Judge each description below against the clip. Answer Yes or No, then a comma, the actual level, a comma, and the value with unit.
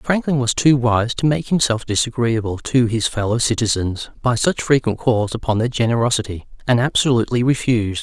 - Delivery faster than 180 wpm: No, average, 165 wpm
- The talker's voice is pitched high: No, low, 120 Hz